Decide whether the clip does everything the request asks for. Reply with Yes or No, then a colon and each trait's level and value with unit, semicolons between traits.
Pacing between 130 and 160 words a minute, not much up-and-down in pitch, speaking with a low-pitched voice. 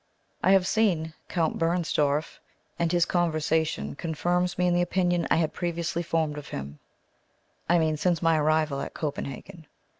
No: average, 155 wpm; narrow, 2.2 semitones; medium, 165 Hz